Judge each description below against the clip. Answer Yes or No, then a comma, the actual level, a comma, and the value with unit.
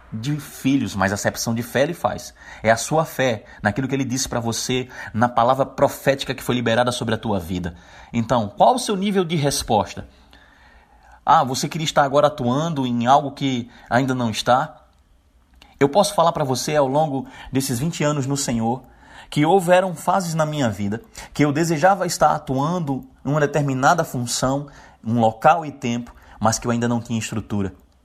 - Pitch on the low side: Yes, low, 130 Hz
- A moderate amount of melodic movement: Yes, average, 4.4 semitones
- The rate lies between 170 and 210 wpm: Yes, fast, 185 wpm